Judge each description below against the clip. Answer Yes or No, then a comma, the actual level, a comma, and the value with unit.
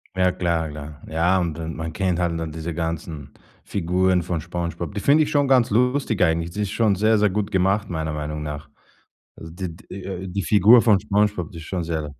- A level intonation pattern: No, average, 3.7 semitones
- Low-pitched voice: Yes, very low, 90 Hz